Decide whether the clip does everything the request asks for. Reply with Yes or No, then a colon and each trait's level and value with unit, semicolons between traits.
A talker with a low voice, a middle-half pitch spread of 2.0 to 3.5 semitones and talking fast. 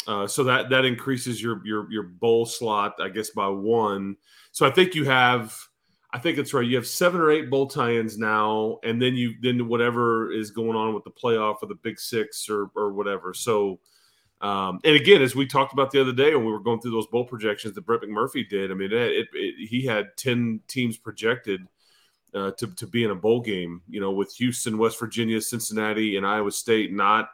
Yes: low, 115 Hz; average, 2.9 semitones; fast, 220 wpm